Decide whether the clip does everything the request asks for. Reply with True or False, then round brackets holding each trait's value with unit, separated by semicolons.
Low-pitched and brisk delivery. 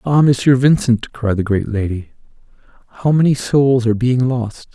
False (125 Hz; 165 wpm)